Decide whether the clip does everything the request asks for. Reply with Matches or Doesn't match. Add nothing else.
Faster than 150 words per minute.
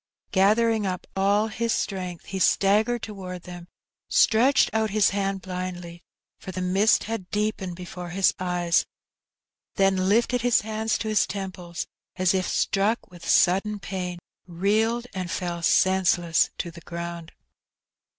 Doesn't match